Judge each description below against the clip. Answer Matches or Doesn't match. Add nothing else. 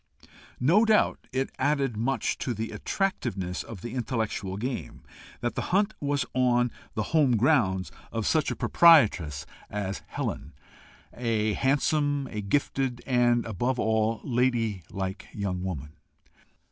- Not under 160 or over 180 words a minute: Doesn't match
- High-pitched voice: Doesn't match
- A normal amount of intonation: Matches